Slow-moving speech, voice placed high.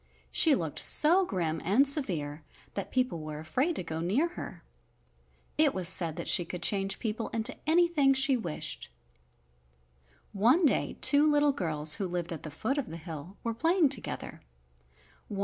No: average, 165 wpm; high, 210 Hz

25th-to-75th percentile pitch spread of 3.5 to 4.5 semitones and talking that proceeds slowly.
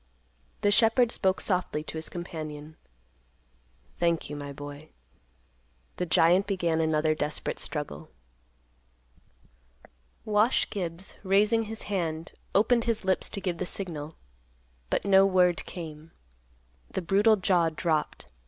Yes: average, 4.0 semitones; slow, 120 wpm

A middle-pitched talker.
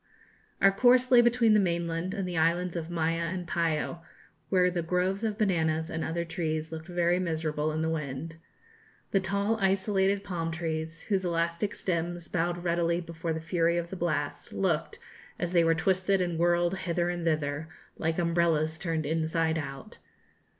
Yes: medium, 170 Hz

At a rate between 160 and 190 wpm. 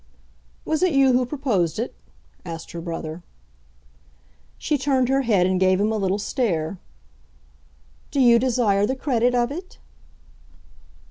No: average, 140 wpm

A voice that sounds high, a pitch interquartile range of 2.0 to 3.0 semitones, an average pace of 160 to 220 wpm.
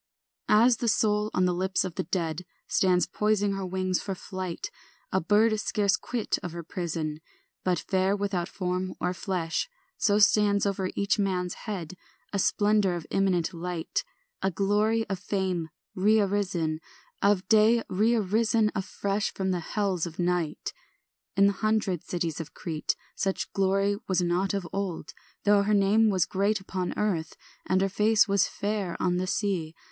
Yes: high, 195 Hz; narrow, 2.5 semitones; average, 165 wpm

